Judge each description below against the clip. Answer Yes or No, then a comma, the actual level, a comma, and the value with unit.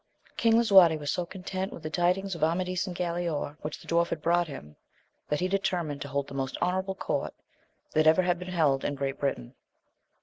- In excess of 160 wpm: Yes, fast, 205 wpm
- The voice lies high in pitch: No, medium, 170 Hz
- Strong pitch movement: No, average, 3.8 semitones